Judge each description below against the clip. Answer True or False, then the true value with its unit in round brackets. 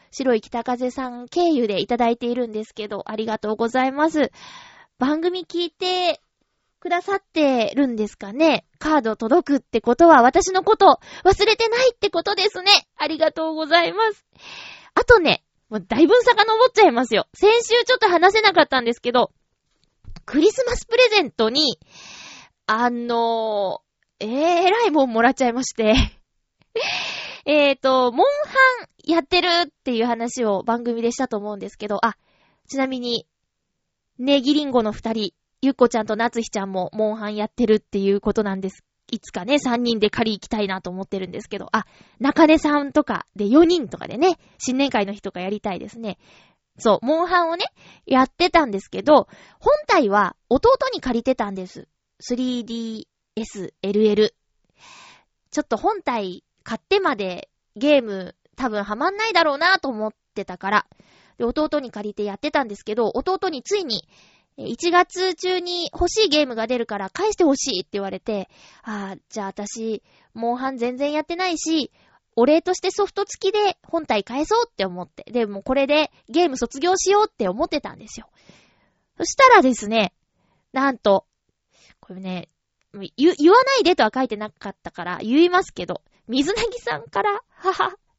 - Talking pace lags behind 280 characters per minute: False (335 characters per minute)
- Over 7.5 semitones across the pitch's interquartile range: True (8.1 semitones)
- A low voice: False (260 Hz)